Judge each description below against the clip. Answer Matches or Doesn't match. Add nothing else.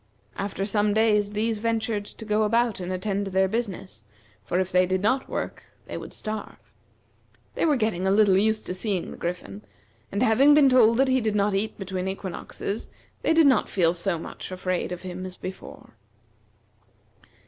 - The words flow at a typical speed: Matches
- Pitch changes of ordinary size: Matches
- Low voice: Doesn't match